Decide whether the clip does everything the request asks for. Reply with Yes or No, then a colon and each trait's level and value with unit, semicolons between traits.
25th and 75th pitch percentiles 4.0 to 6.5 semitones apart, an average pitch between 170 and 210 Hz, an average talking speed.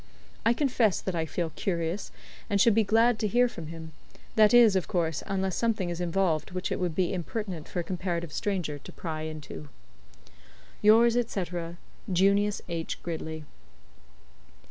Yes: average, 4.3 semitones; medium, 185 Hz; average, 160 wpm